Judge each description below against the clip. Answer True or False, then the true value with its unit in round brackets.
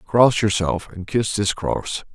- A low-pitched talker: True (100 Hz)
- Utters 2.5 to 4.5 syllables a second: True (3.6 syllables/s)